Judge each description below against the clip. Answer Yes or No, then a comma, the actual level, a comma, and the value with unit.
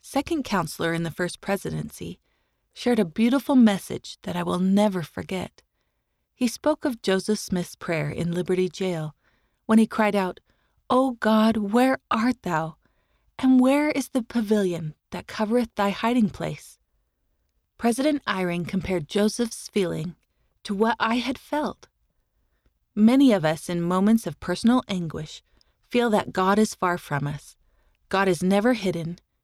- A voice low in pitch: No, high, 200 Hz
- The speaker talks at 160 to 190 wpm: No, average, 150 wpm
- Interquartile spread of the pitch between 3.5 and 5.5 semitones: Yes, average, 5.2 semitones